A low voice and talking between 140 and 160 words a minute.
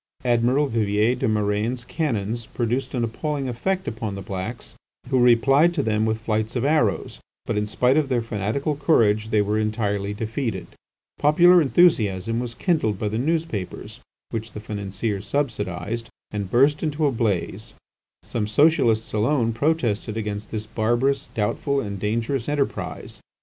Yes: low, 115 Hz; average, 150 wpm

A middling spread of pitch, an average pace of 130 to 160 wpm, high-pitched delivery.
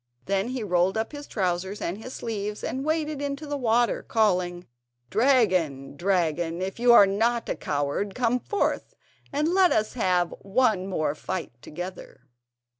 No: wide, 5.8 semitones; average, 155 wpm; high, 205 Hz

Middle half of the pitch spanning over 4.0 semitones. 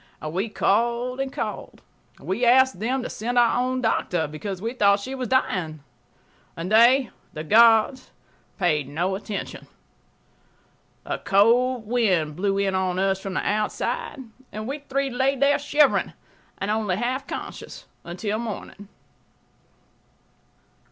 Yes: average, 4.7 semitones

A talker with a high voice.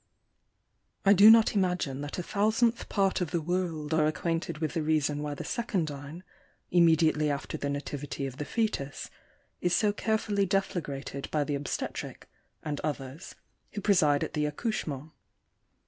No: medium, 160 Hz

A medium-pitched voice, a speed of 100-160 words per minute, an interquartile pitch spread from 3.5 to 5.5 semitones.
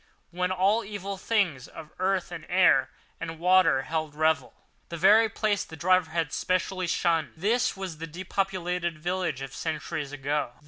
No: medium, 175 Hz; average, 155 wpm; average, 3.1 semitones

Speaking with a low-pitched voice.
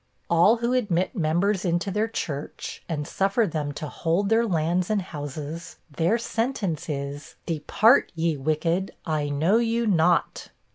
No: medium, 170 Hz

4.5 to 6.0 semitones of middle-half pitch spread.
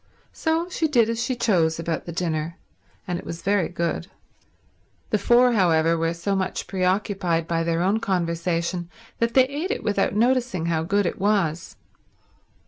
Yes: average, 5.2 semitones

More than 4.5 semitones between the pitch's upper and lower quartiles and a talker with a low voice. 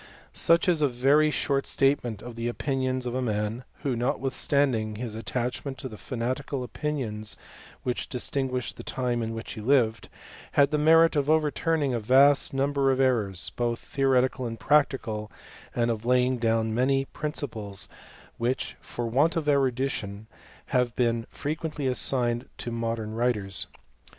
No: average, 3.2 semitones; low, 125 Hz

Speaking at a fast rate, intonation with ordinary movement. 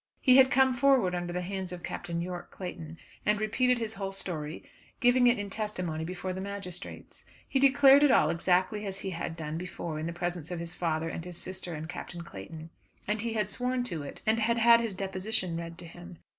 Yes: fast, 215 wpm; average, 4.7 semitones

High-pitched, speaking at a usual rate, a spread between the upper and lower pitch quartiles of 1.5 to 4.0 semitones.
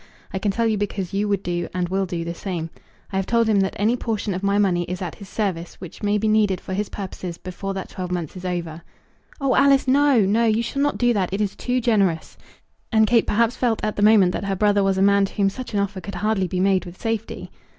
No: high, 200 Hz; fast, 260 wpm; average, 2.9 semitones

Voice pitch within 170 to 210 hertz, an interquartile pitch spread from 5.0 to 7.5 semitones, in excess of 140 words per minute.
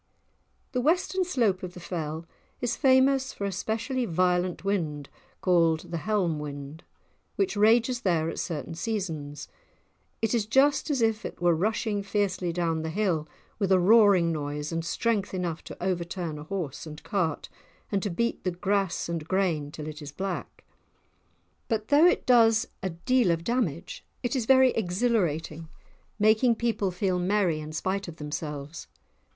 Yes: medium, 185 Hz; wide, 5.4 semitones; average, 160 wpm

